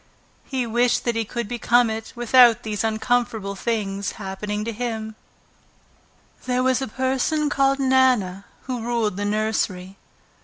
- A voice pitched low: No, high, 230 Hz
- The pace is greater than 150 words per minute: No, average, 140 wpm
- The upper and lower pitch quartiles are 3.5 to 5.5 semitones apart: No, average, 3.1 semitones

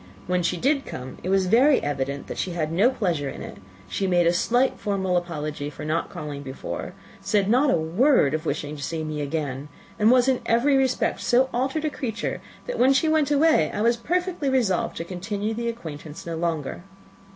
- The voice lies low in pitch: No, high, 190 Hz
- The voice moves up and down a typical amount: No, wide, 8.5 semitones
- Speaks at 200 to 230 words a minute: Yes, fast, 205 wpm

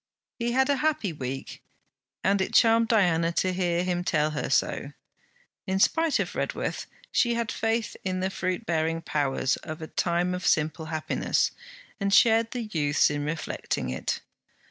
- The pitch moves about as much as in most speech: No, wide, 6.0 semitones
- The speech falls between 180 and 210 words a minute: No, average, 165 wpm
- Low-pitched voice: No, medium, 180 Hz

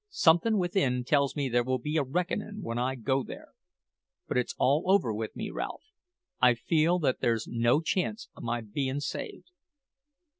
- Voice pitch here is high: No, medium, 140 Hz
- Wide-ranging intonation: Yes, wide, 6.4 semitones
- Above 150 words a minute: Yes, average, 175 wpm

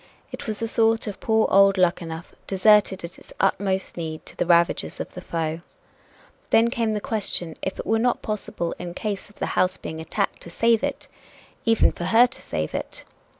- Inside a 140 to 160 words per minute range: No, average, 195 wpm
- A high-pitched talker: Yes, high, 195 Hz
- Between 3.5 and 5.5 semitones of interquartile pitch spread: Yes, average, 4.4 semitones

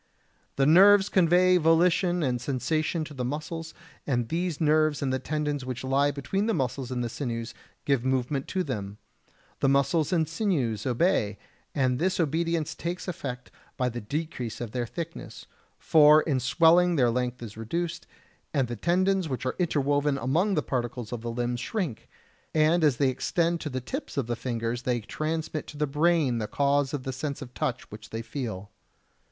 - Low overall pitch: No, medium, 145 Hz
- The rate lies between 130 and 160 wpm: No, average, 180 wpm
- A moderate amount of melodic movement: Yes, average, 4.9 semitones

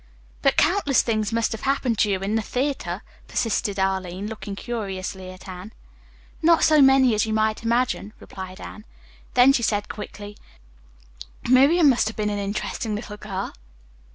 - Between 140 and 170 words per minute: Yes, average, 160 wpm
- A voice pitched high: Yes, high, 215 Hz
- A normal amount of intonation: Yes, average, 3.7 semitones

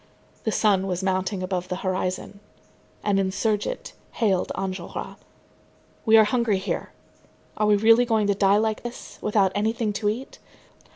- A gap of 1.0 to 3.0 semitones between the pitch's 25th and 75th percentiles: Yes, narrow, 2.6 semitones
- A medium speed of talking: Yes, average, 150 wpm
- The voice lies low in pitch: No, high, 205 Hz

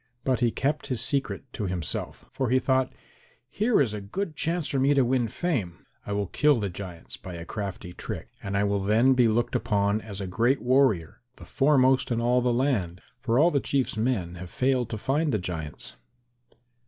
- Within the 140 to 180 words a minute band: No, fast, 205 wpm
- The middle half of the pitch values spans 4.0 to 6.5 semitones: Yes, average, 5.0 semitones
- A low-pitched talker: Yes, low, 120 Hz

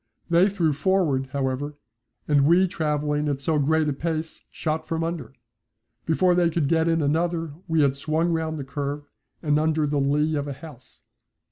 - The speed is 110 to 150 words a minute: No, average, 175 wpm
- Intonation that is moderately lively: No, narrow, 2.3 semitones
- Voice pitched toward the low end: No, medium, 155 Hz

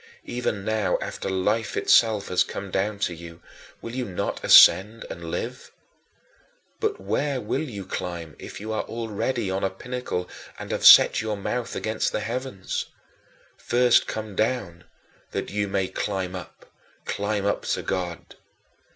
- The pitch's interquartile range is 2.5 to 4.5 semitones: Yes, average, 3.4 semitones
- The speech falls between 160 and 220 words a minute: No, average, 150 wpm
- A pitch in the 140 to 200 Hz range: No, low, 105 Hz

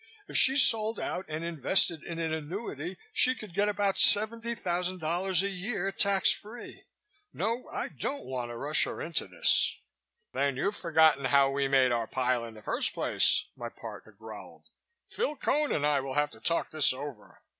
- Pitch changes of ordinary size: No, wide, 6.7 semitones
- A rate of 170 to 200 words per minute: Yes, average, 175 wpm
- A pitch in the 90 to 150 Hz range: No, medium, 170 Hz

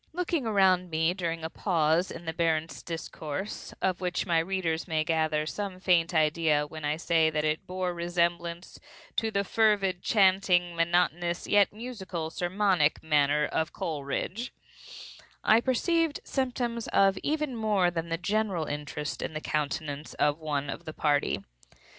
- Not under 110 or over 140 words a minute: No, average, 150 wpm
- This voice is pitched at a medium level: Yes, medium, 170 Hz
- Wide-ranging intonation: No, average, 3.7 semitones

